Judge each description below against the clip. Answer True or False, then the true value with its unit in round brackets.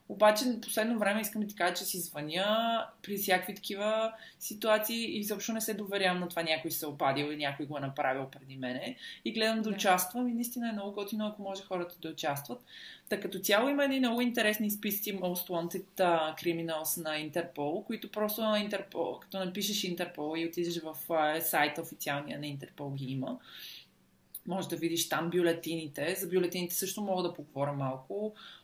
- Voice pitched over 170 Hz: True (185 Hz)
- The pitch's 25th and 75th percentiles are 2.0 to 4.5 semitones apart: False (5.1 semitones)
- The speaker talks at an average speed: False (180 wpm)